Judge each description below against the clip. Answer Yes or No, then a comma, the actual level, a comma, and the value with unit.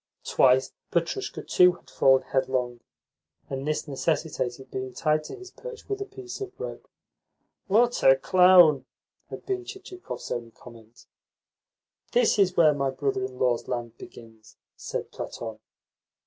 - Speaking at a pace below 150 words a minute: Yes, average, 140 wpm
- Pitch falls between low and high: Yes, medium, 145 Hz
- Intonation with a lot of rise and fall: Yes, wide, 7.9 semitones